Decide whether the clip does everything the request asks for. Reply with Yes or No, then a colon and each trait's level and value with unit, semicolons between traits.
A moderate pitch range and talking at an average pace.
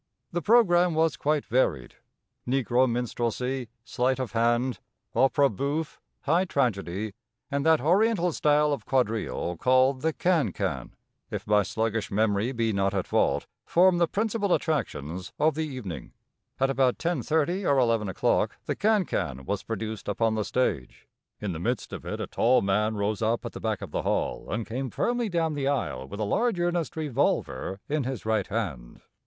No: wide, 6.5 semitones; average, 170 wpm